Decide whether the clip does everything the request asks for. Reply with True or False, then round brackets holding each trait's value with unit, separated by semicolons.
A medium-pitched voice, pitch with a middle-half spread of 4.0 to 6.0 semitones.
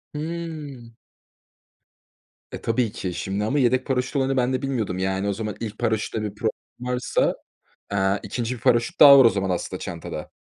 False (115 Hz; 4.5 semitones)